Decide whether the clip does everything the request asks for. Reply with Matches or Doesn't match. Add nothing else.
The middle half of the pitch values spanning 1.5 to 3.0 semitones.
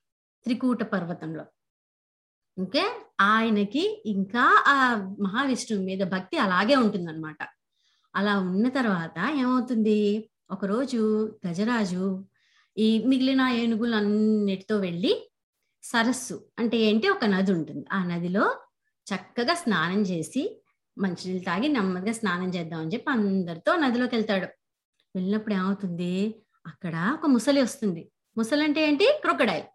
Doesn't match